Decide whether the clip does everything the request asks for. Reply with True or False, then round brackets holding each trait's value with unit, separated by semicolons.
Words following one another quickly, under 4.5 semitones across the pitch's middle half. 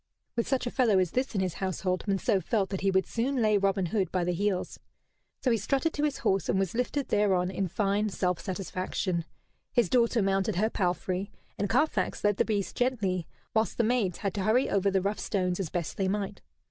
True (215 wpm; 3.1 semitones)